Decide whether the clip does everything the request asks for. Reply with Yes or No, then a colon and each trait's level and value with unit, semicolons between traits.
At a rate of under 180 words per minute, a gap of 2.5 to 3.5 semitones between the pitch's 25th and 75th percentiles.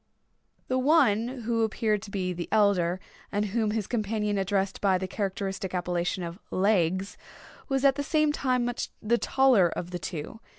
No: average, 170 wpm; average, 4.2 semitones